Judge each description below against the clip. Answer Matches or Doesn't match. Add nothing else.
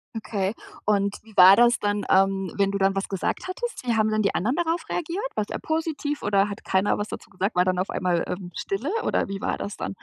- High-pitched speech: Matches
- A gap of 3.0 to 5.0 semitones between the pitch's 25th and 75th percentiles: Matches